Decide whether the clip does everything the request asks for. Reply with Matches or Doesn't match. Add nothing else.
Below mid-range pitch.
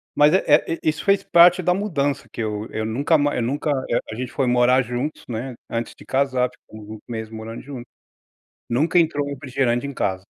Matches